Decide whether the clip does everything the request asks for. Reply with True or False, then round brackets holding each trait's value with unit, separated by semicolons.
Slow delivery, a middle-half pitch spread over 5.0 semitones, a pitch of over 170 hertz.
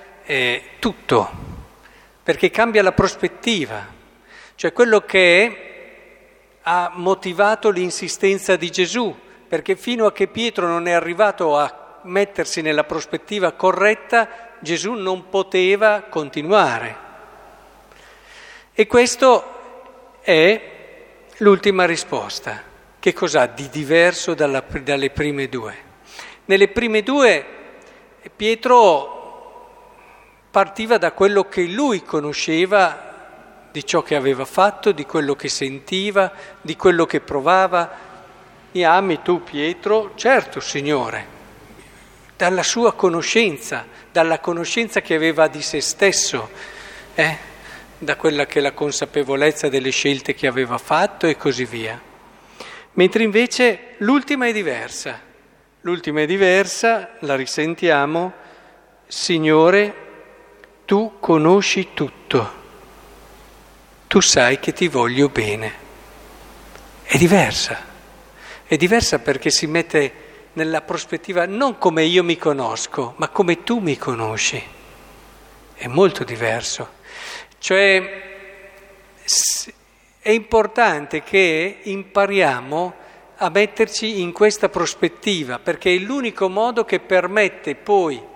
True (105 wpm; 5.4 semitones; 185 Hz)